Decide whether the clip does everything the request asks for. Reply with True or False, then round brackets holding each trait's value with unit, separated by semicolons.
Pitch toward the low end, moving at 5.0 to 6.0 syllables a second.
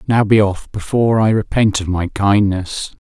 False (105 Hz; 4.6 syllables/s)